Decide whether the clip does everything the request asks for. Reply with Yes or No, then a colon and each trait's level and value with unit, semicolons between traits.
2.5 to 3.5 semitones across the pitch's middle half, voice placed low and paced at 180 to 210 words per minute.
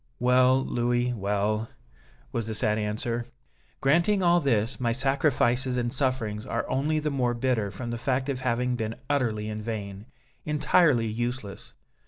No: average, 3.2 semitones; low, 120 Hz; average, 150 wpm